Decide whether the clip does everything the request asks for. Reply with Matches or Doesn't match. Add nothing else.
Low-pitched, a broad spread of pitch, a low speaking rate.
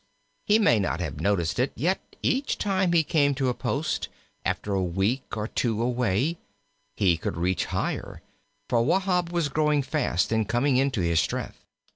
Doesn't match